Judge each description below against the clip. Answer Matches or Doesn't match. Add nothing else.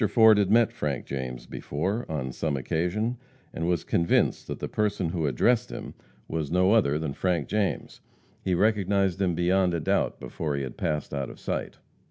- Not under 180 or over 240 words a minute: Matches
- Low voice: Matches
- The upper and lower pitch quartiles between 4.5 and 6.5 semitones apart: Matches